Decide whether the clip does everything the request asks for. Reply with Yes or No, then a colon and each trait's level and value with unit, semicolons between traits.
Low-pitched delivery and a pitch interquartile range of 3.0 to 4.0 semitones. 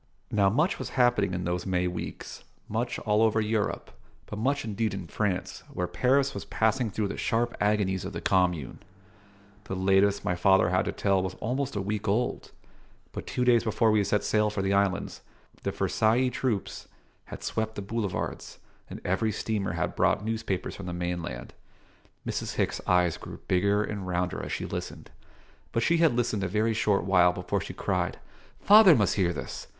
Yes: low, 105 Hz; average, 3.3 semitones